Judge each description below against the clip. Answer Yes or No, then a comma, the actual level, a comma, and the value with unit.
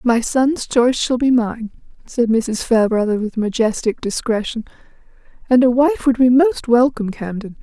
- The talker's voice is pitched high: Yes, high, 240 Hz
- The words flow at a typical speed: Yes, average, 155 wpm